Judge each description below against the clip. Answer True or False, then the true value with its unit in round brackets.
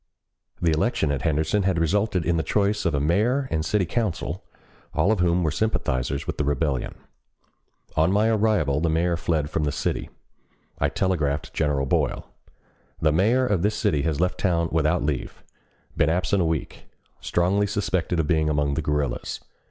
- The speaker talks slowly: False (175 wpm)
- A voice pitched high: False (80 Hz)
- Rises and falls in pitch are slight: False (4.6 semitones)